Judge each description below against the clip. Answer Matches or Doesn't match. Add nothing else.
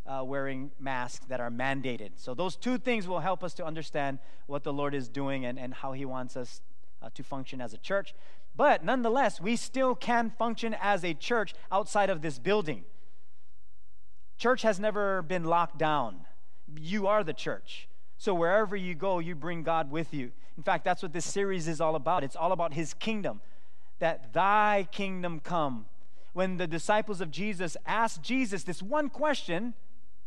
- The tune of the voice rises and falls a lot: Matches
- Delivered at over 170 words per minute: Matches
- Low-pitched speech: Doesn't match